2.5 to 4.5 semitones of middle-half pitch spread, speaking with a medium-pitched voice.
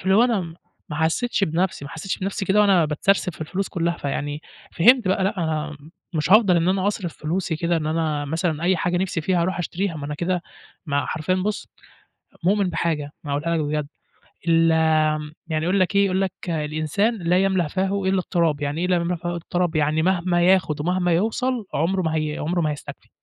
Yes: average, 3.3 semitones; medium, 175 Hz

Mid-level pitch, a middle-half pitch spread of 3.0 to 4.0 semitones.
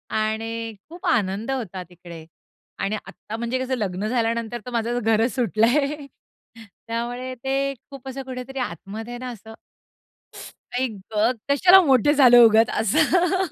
No: high, 235 Hz; average, 3.4 semitones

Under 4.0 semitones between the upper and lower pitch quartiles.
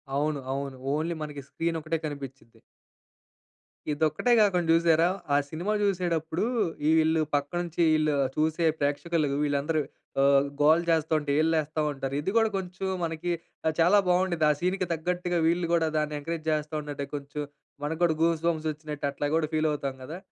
Yes: narrow, 2.4 semitones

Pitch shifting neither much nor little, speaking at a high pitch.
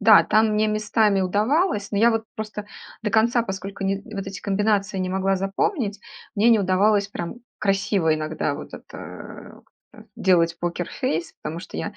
No: narrow, 2.3 semitones; high, 200 Hz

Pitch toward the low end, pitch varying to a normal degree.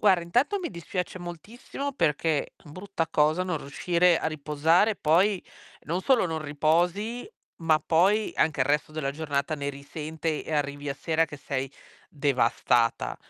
No: medium, 160 Hz; average, 3.7 semitones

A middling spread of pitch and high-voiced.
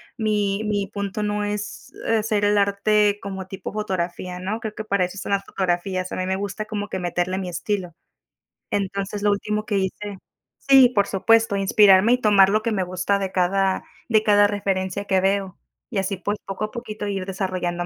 No: narrow, 1.8 semitones; high, 200 Hz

